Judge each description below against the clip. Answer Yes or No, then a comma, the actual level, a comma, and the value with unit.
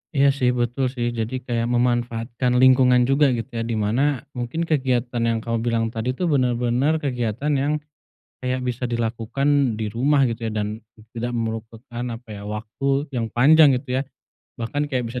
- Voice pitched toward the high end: No, low, 120 Hz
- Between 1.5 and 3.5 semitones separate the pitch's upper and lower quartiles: Yes, narrow, 2.4 semitones